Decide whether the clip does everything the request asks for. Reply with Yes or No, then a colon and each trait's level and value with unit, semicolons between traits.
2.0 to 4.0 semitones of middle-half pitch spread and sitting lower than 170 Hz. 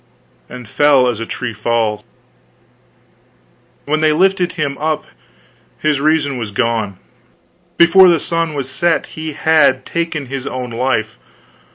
No: average, 4.8 semitones; medium, 140 Hz